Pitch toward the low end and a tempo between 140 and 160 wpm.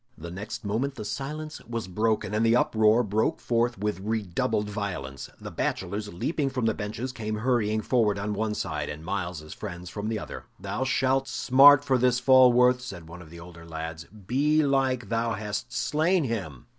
No: low, 110 Hz; average, 180 wpm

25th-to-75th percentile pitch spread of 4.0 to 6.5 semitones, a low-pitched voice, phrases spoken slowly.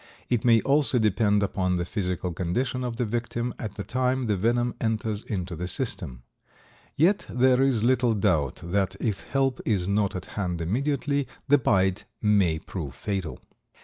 No: average, 5.2 semitones; low, 105 Hz; average, 165 wpm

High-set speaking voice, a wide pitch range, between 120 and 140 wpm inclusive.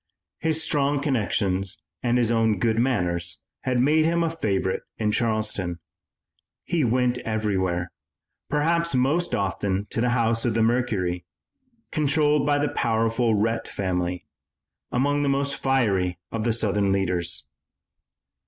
No: low, 115 Hz; wide, 6.0 semitones; slow, 135 wpm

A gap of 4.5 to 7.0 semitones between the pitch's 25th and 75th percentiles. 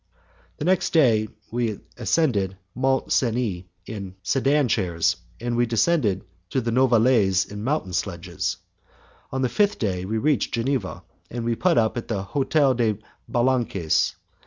Yes: average, 4.8 semitones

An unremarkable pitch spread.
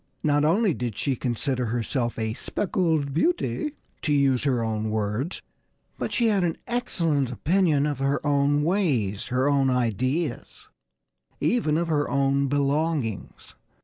Yes: average, 4.5 semitones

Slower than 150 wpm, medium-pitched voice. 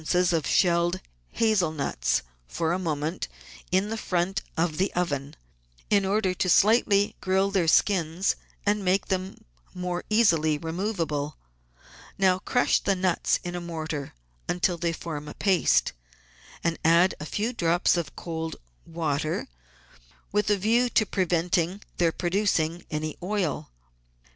Yes: slow, 135 wpm; medium, 175 Hz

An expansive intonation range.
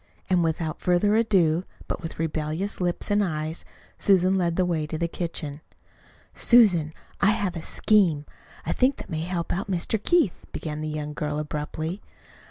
No: average, 3.7 semitones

